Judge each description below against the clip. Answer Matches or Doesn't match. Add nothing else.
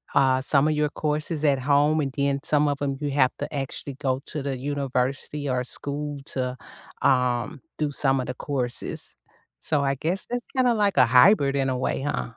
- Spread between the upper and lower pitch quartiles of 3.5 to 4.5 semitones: Doesn't match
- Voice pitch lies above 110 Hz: Matches